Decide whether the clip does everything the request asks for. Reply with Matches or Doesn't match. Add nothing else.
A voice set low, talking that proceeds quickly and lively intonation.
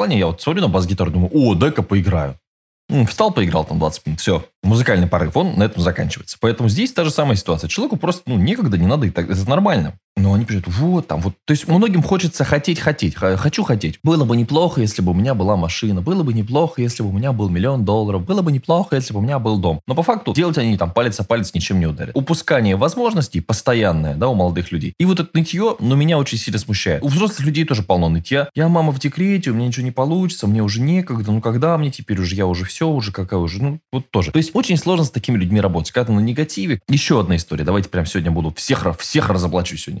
Matches